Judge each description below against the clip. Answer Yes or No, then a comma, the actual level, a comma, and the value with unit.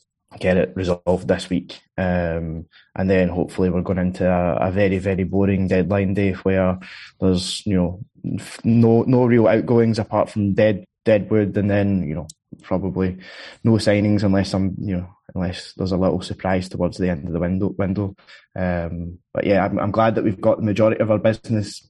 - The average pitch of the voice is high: No, very low, 95 Hz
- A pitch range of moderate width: No, narrow, 2.3 semitones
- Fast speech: No, average, 190 wpm